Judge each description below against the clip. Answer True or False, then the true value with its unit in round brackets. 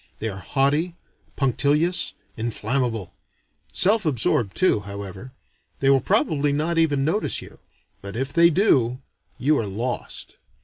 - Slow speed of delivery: True (130 wpm)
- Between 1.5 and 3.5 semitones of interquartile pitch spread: False (5.6 semitones)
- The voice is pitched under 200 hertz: True (135 Hz)